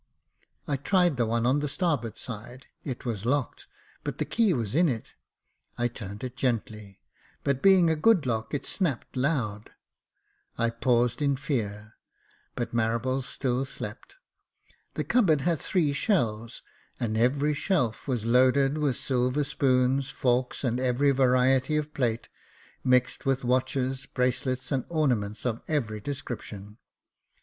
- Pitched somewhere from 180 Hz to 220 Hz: No, low, 130 Hz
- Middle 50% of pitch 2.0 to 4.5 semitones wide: Yes, average, 3.4 semitones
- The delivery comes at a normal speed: Yes, average, 145 wpm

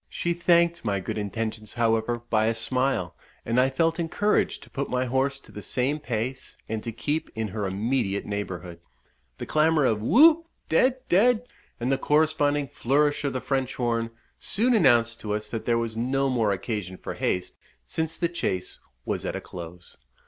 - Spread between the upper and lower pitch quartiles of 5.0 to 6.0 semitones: Yes, wide, 5.6 semitones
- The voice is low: Yes, low, 125 Hz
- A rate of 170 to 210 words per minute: Yes, average, 180 wpm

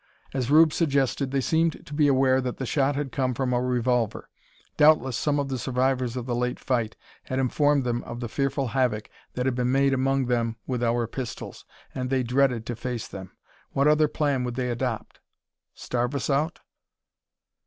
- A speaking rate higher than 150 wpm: Yes, average, 190 wpm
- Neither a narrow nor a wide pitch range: No, narrow, 2.1 semitones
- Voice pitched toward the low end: Yes, low, 130 Hz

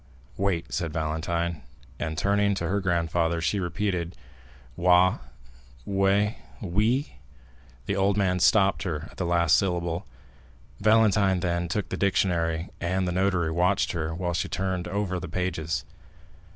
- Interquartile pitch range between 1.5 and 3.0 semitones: Yes, average, 2.7 semitones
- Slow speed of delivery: Yes, slow, 130 wpm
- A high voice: No, very low, 90 Hz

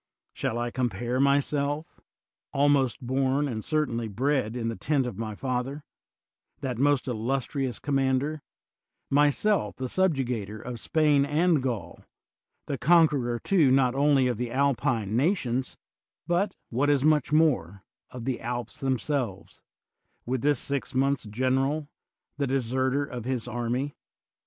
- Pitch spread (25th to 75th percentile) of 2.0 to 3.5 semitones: Yes, average, 3.1 semitones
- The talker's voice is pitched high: No, low, 130 Hz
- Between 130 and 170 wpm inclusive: Yes, slow, 135 wpm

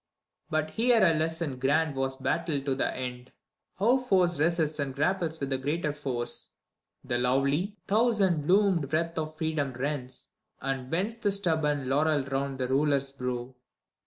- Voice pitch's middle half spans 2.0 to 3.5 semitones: No, average, 4.0 semitones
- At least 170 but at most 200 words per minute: No, average, 155 wpm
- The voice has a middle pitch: Yes, medium, 150 Hz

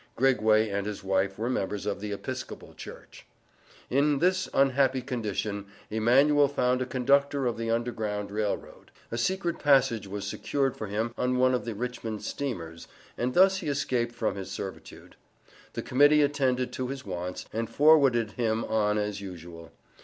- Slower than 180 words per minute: Yes, average, 165 wpm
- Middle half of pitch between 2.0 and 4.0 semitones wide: No, average, 4.6 semitones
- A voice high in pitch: No, low, 120 Hz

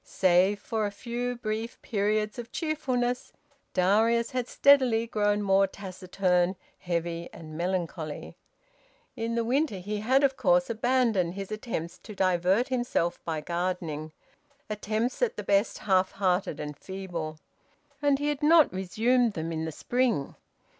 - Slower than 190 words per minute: Yes, average, 140 wpm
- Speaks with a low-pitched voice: No, high, 205 Hz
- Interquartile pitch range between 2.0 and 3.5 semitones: No, average, 5.2 semitones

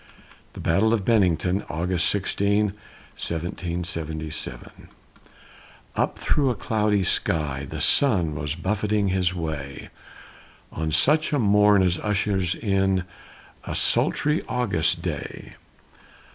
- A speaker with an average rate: No, slow, 105 wpm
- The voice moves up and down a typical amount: Yes, average, 4.2 semitones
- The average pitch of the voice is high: No, very low, 95 Hz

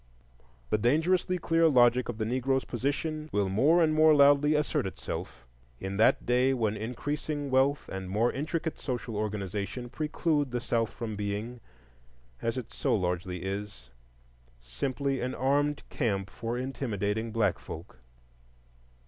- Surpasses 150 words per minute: No, average, 140 wpm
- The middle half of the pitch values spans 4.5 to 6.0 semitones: Yes, wide, 5.6 semitones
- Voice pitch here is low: Yes, low, 120 Hz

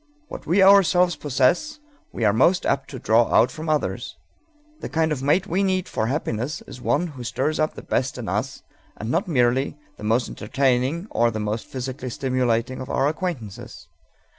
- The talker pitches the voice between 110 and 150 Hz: Yes, low, 135 Hz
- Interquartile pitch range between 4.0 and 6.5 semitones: Yes, average, 5.1 semitones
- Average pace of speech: Yes, average, 185 wpm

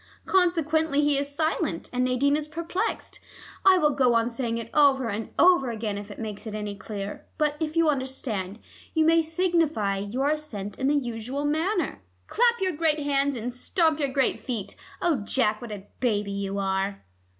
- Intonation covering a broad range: Yes, wide, 6.5 semitones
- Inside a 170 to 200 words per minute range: Yes, average, 185 wpm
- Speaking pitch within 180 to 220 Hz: No, very high, 270 Hz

